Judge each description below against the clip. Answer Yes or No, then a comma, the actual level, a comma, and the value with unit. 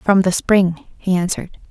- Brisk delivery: No, average, 175 wpm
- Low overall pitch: No, medium, 185 Hz